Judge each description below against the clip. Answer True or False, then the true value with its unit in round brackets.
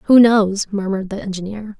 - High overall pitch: True (205 Hz)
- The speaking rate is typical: True (165 wpm)